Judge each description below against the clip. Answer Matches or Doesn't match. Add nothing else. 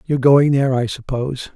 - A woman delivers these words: Doesn't match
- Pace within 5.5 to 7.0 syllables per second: Matches